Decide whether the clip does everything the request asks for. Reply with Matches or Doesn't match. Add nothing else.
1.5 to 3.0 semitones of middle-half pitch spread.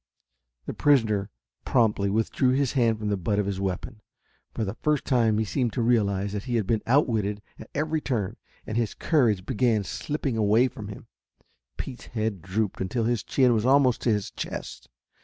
Doesn't match